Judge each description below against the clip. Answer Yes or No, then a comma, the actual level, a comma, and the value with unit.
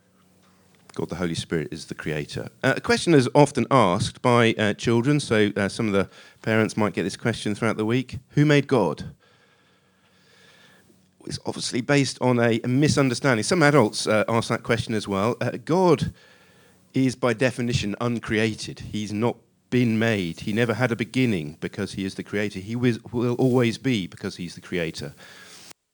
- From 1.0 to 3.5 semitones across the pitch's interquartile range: Yes, average, 3.2 semitones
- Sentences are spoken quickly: No, average, 175 wpm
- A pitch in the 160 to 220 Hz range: No, low, 115 Hz